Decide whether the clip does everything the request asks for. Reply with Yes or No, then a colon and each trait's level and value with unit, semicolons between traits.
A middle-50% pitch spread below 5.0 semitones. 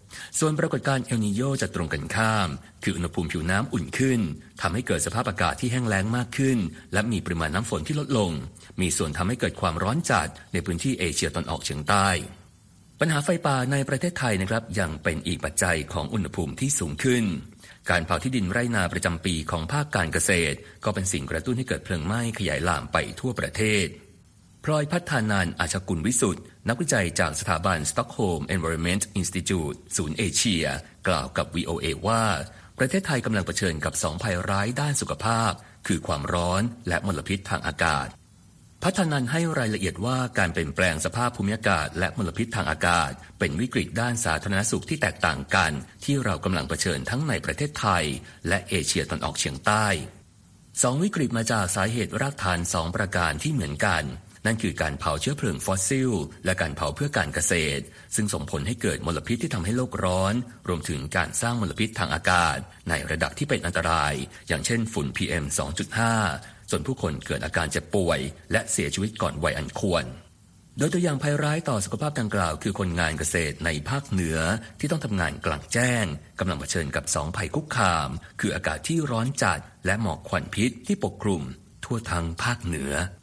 No: wide, 5.5 semitones